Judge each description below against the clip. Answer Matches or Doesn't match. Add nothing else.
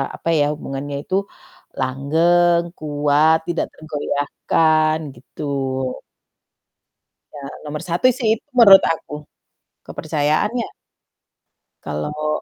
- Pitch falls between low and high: Matches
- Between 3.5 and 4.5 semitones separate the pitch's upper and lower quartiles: Doesn't match